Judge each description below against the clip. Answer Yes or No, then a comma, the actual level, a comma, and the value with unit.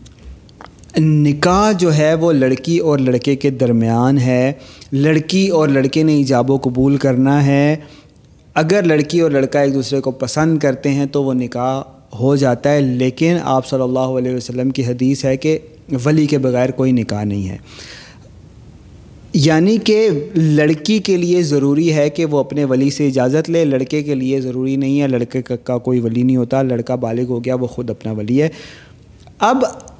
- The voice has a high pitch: No, low, 135 Hz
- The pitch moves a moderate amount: Yes, average, 3.0 semitones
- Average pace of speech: Yes, average, 175 wpm